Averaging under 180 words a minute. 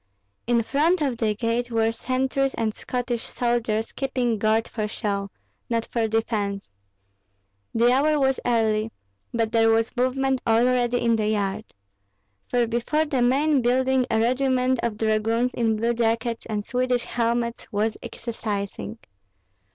Yes: average, 140 wpm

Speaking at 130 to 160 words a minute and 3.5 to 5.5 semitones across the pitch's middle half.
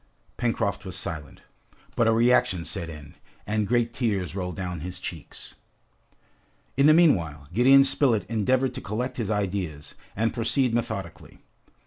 Yes: average, 140 wpm; average, 5.1 semitones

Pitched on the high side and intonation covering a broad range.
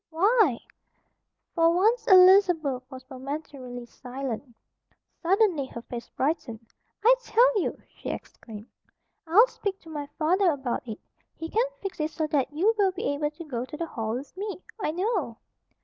Yes: very high, 315 Hz; wide, 6.7 semitones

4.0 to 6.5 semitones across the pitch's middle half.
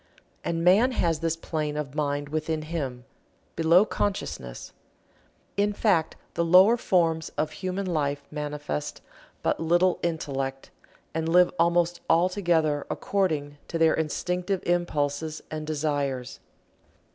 No: average, 3.0 semitones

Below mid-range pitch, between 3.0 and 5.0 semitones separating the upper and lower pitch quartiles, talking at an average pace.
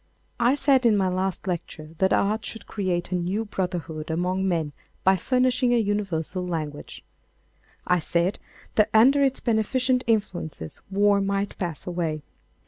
No: high, 190 Hz; average, 4.1 semitones; average, 145 wpm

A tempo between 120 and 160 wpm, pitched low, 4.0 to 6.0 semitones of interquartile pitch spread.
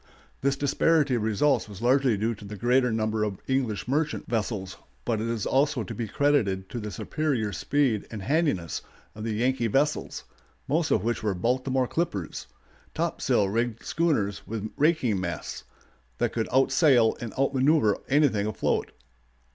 Yes: average, 155 wpm; low, 120 Hz; average, 4.4 semitones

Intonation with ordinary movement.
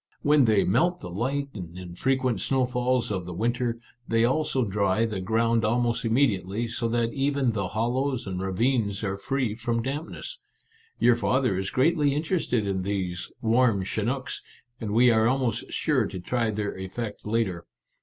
Yes: average, 4.3 semitones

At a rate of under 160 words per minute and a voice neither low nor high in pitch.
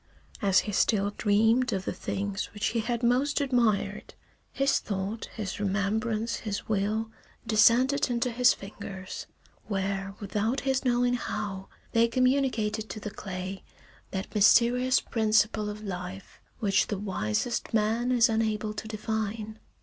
No: average, 140 wpm; high, 215 Hz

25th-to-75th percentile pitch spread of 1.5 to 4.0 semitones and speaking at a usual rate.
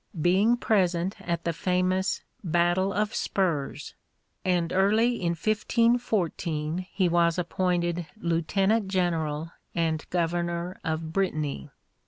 No: narrow, 2.5 semitones; slow, 105 wpm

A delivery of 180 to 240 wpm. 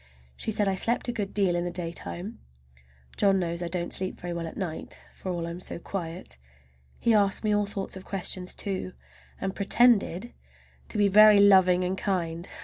Yes: average, 190 wpm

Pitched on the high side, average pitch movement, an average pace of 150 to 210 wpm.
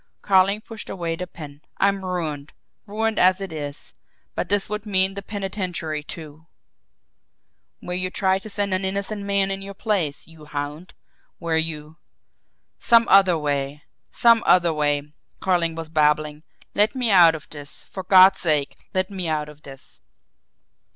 No: medium, 180 Hz; average, 4.4 semitones; average, 165 wpm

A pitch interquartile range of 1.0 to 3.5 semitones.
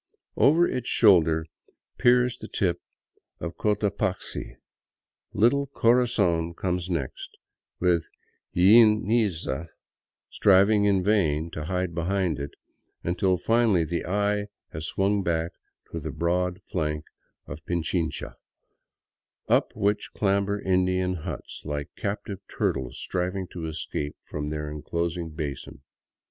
No: average, 3.9 semitones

